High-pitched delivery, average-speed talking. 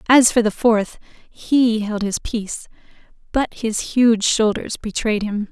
Yes: high, 220 Hz; average, 150 wpm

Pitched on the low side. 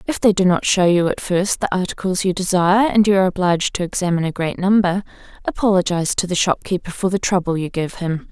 No: medium, 185 Hz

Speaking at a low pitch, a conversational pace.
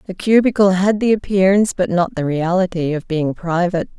No: medium, 185 Hz; average, 180 wpm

